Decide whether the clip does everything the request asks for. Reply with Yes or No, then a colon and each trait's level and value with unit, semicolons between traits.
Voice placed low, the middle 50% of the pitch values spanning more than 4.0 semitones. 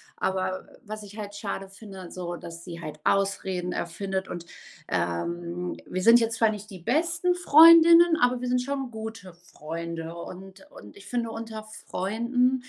No: high, 195 Hz; average, 5.1 semitones